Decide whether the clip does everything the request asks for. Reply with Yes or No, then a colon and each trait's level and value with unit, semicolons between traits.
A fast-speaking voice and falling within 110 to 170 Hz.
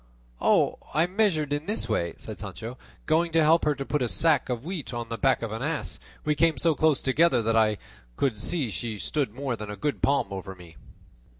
Yes: fast, 215 wpm; low, 135 Hz